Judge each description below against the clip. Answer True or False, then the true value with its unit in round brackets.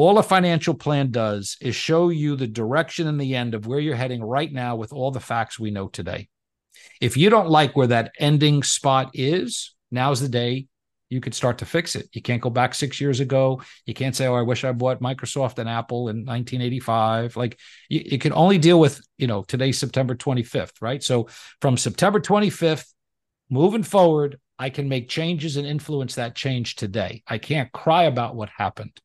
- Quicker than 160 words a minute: True (200 wpm)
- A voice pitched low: True (130 Hz)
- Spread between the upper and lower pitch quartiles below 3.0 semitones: False (3.8 semitones)